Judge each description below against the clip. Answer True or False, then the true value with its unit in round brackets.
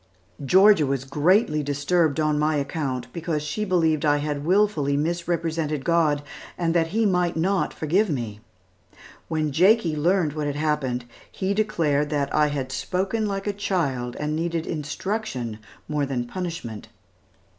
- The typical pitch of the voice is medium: True (155 Hz)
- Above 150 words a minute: False (145 wpm)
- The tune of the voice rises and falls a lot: False (3.7 semitones)